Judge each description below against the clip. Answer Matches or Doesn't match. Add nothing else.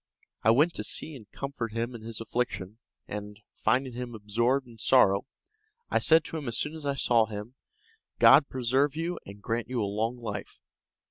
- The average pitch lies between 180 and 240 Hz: Doesn't match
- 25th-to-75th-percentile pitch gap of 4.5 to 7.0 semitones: Doesn't match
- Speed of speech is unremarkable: Matches